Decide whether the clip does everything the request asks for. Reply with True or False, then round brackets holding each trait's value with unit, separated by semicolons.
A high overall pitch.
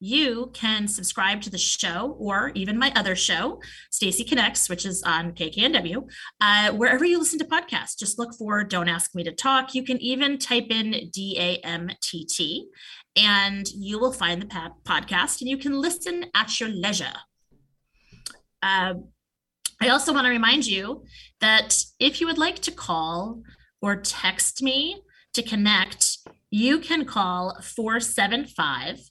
True (215 Hz)